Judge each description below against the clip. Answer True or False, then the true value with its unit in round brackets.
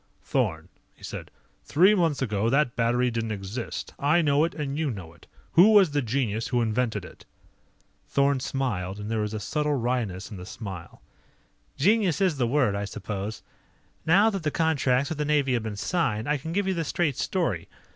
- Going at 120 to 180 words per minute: False (195 wpm)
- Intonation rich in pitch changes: True (6.3 semitones)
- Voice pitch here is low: True (130 Hz)